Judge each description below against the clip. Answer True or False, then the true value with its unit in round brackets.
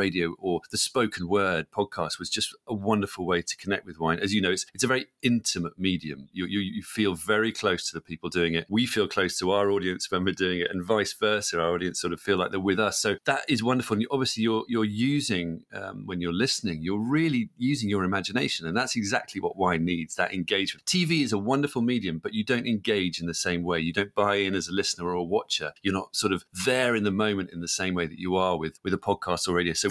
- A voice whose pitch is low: True (95 Hz)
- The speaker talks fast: True (260 wpm)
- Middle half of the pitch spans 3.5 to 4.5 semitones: True (4.1 semitones)